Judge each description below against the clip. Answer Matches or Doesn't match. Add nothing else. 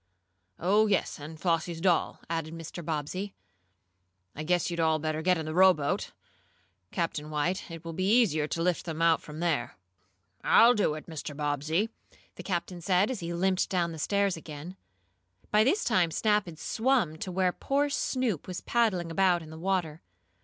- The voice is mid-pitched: Matches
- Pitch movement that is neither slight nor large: Matches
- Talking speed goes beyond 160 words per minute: Matches